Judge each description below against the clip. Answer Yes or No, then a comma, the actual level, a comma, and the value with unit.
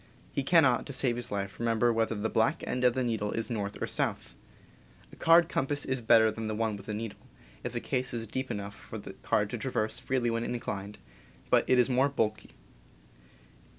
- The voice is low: Yes, low, 115 Hz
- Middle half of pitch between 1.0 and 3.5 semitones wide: Yes, average, 2.8 semitones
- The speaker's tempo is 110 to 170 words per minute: No, fast, 205 wpm